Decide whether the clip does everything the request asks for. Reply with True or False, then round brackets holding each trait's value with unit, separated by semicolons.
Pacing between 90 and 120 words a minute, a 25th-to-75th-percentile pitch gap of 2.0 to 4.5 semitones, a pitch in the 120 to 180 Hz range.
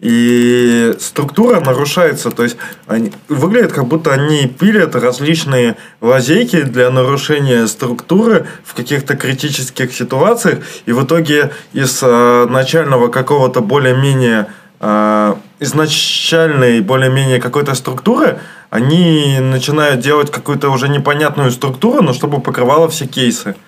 True (110 wpm; 3.2 semitones; 135 Hz)